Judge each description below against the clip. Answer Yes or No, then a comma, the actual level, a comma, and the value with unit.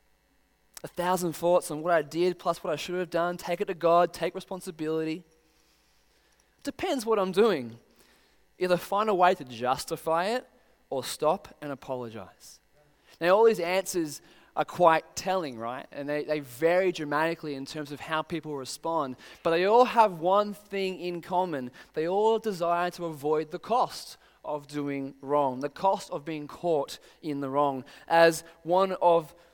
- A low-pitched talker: No, medium, 170 Hz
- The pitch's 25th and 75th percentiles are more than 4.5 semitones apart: No, average, 3.8 semitones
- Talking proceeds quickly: No, average, 165 wpm